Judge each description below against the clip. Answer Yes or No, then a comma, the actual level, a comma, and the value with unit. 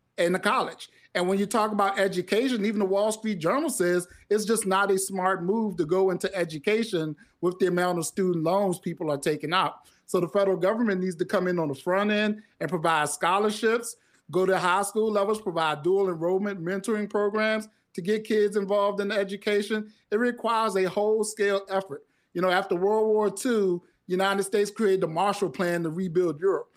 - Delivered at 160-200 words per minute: Yes, average, 195 wpm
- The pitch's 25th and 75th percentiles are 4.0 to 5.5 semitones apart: No, average, 2.7 semitones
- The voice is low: No, high, 195 Hz